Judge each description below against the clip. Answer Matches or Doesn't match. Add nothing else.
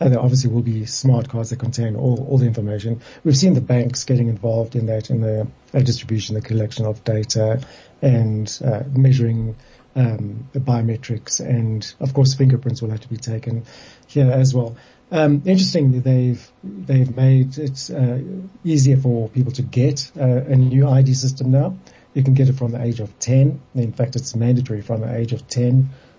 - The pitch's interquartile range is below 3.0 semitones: Matches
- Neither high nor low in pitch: Doesn't match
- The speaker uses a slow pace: Doesn't match